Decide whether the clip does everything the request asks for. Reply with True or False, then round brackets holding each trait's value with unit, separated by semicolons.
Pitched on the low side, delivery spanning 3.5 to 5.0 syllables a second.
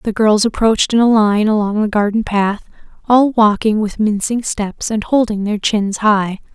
False (215 Hz; 4.5 syllables/s)